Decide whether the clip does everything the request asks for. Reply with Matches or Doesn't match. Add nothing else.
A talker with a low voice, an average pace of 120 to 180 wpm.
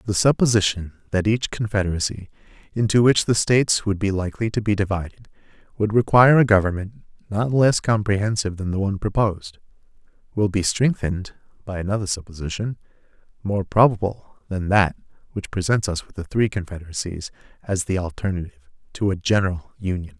Matches